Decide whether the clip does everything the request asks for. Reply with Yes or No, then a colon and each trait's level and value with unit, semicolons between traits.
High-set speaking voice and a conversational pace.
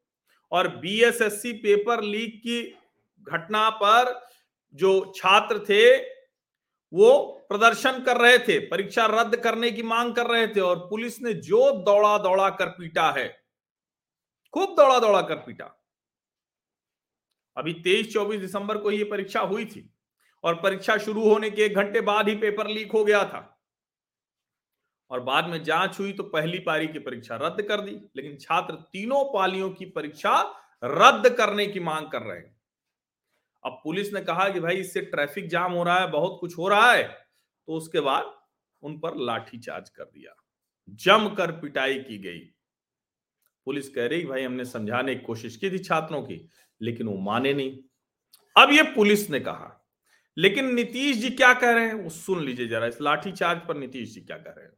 Yes: high, 195 Hz; average, 175 wpm